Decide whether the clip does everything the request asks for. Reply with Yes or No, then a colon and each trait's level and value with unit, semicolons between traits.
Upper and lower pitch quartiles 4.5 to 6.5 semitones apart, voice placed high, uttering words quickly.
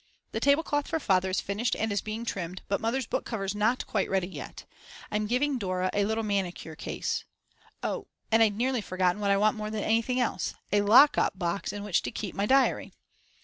No: average, 3.1 semitones; high, 210 Hz; fast, 215 wpm